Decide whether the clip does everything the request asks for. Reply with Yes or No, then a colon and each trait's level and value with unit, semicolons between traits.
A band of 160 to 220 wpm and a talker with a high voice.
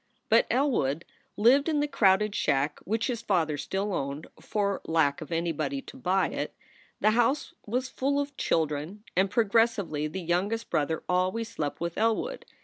Yes: average, 165 wpm; high, 200 Hz